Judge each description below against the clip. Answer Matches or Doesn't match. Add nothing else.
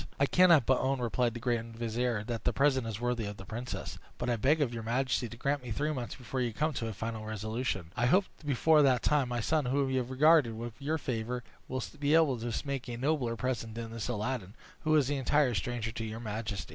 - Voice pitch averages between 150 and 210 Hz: Doesn't match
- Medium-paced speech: Doesn't match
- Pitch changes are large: Doesn't match